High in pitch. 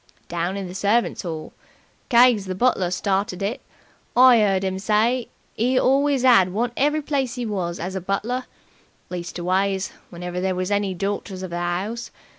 Yes: high, 200 Hz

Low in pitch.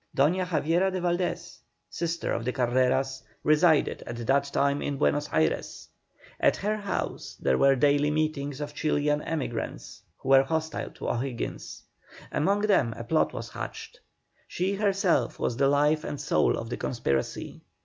No: medium, 145 Hz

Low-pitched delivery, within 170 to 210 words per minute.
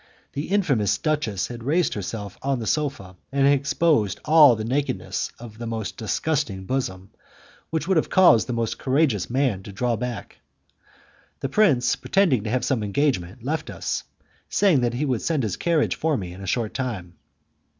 Yes: low, 125 Hz; average, 175 wpm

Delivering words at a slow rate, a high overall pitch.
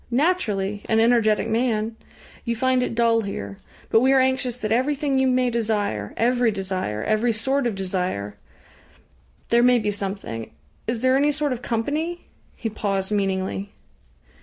No: average, 155 wpm; high, 225 Hz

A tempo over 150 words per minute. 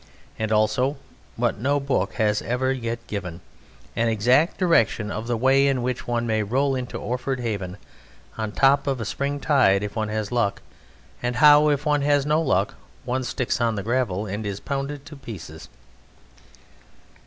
Yes: average, 175 wpm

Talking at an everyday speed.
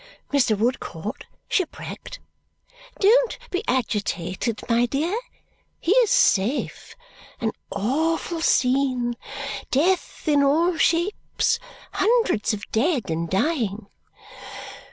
No: slow, 90 wpm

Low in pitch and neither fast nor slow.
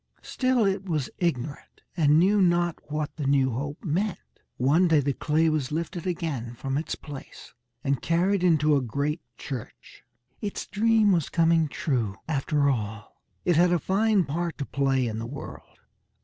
No: medium, 155 Hz; average, 165 wpm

